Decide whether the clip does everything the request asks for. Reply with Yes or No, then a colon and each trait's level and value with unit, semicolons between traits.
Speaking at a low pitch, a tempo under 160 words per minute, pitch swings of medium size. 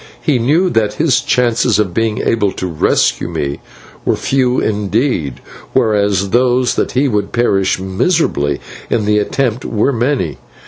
Yes: low, 115 Hz; average, 145 wpm; average, 4.4 semitones